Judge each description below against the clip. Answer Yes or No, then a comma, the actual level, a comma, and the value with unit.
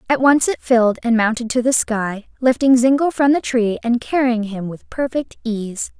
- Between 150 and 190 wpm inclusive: No, average, 200 wpm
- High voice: Yes, high, 240 Hz